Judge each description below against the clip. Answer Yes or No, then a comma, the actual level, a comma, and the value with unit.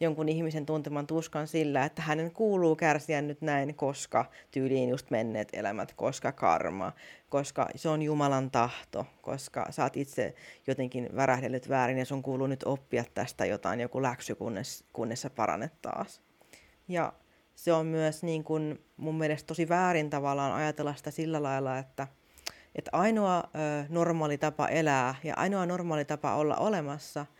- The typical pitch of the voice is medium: Yes, medium, 150 Hz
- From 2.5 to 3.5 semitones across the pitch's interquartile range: Yes, average, 2.8 semitones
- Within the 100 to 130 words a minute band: No, fast, 155 wpm